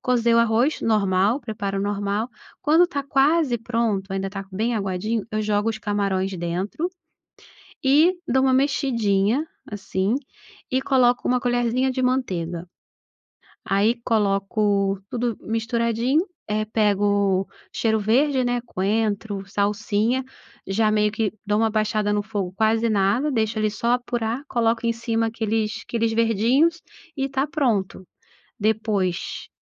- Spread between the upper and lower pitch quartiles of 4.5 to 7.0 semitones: No, average, 3.1 semitones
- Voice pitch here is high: Yes, high, 220 Hz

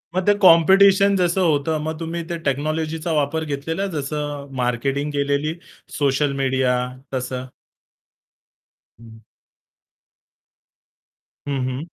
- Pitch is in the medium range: Yes, medium, 150 Hz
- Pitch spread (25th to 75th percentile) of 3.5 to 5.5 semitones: No, average, 3.0 semitones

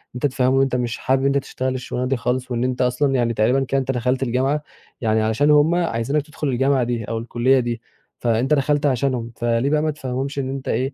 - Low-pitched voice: Yes, low, 130 Hz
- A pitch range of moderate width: No, narrow, 2.3 semitones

